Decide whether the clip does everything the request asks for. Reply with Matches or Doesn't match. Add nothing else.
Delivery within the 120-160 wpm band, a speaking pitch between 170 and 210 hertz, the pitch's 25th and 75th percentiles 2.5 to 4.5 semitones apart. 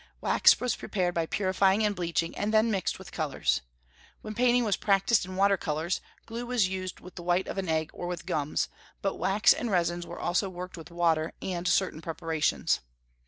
Doesn't match